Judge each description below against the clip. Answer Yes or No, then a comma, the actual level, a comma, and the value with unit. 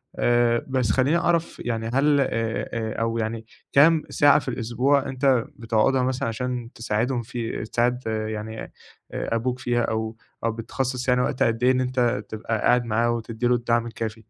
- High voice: No, low, 120 Hz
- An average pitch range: No, narrow, 2.2 semitones